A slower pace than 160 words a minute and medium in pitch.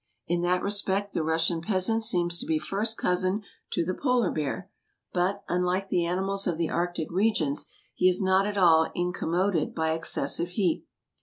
No: average, 170 wpm; medium, 180 Hz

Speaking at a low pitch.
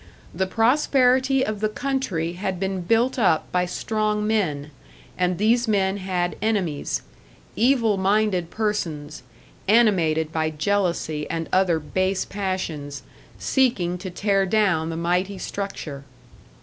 No: high, 190 Hz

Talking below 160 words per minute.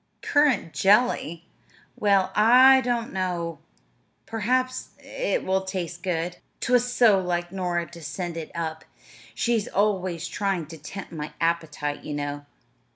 Yes: slow, 135 wpm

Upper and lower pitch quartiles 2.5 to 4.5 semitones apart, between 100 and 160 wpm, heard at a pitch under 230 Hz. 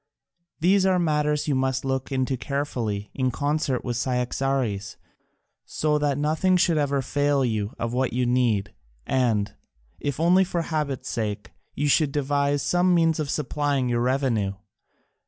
Yes: average, 3.3 semitones; average, 150 wpm; low, 135 Hz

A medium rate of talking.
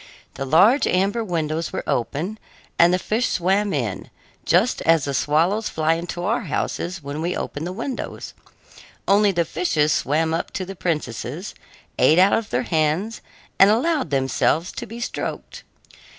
Yes: average, 160 wpm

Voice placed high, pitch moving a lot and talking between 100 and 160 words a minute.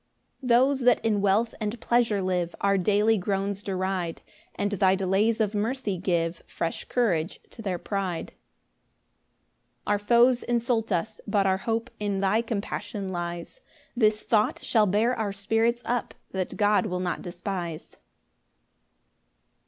No: high, 205 Hz; average, 3.1 semitones; average, 145 wpm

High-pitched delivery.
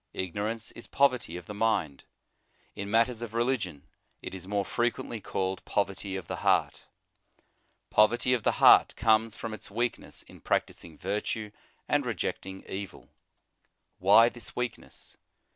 No: low, 105 Hz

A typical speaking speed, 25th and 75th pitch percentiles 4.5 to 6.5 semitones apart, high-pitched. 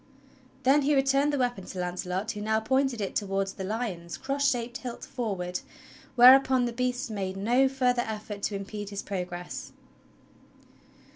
Yes: average, 155 wpm; average, 4.8 semitones; high, 225 Hz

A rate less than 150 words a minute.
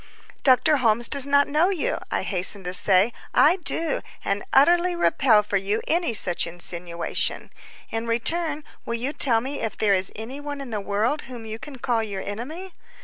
No: average, 185 wpm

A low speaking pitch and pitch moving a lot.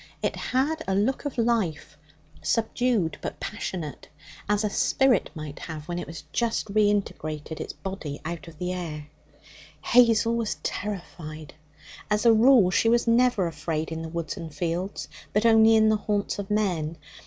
No: high, 195 Hz; wide, 5.7 semitones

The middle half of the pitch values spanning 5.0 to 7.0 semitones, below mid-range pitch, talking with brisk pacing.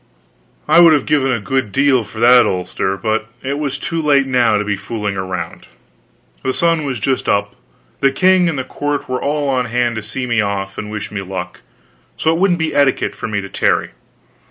Yes: wide, 5.5 semitones; low, 125 Hz; fast, 210 wpm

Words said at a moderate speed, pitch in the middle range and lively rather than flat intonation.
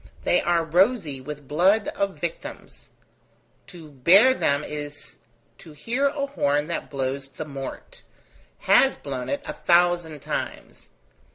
No: slow, 130 wpm; medium, 165 Hz; wide, 5.9 semitones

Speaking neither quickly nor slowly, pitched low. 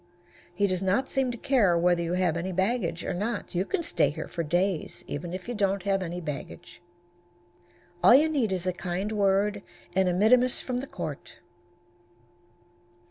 No: average, 180 wpm; high, 190 Hz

